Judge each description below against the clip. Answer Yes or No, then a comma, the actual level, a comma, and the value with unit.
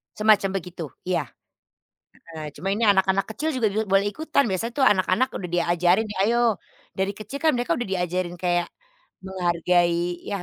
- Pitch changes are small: No, average, 3.7 semitones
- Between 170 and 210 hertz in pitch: Yes, high, 190 Hz